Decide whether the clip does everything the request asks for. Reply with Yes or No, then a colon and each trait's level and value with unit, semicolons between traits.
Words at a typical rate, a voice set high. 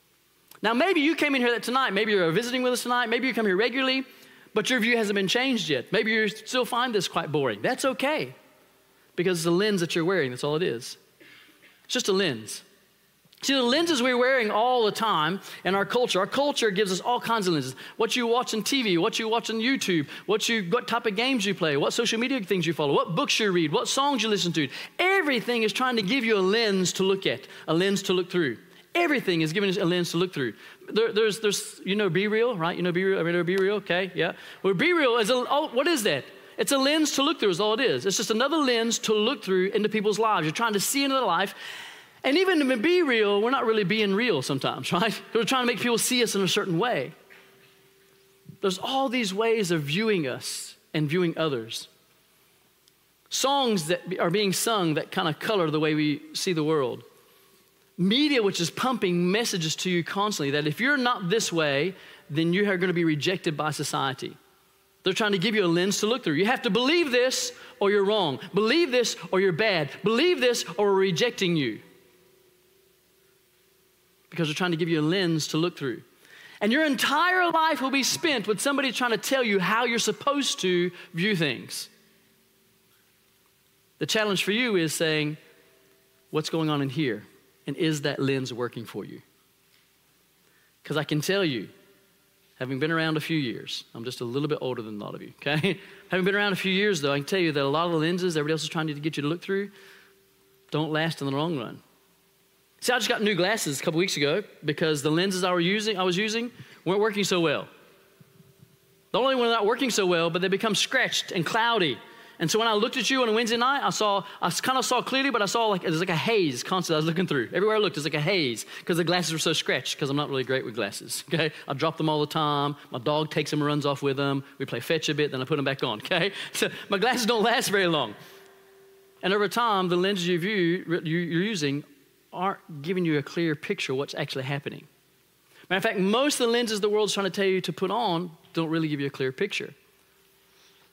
No: fast, 235 wpm; high, 195 Hz